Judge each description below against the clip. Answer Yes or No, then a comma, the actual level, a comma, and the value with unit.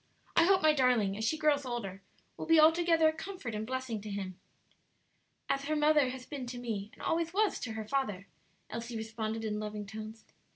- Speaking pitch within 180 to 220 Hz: No, high, 245 Hz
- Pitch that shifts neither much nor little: No, wide, 6.1 semitones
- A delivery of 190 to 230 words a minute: Yes, average, 200 wpm